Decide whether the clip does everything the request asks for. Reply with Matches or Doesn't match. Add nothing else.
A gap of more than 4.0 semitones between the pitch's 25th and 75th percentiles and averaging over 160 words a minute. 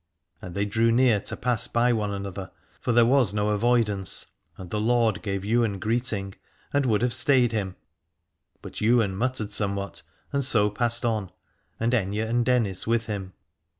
Doesn't match